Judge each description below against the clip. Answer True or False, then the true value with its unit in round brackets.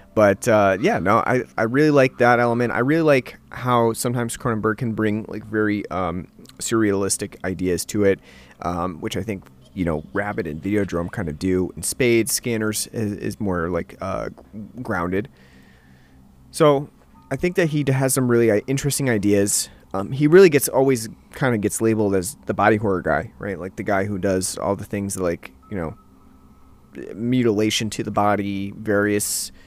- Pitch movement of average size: True (4.5 semitones)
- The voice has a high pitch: False (105 Hz)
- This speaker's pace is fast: False (175 wpm)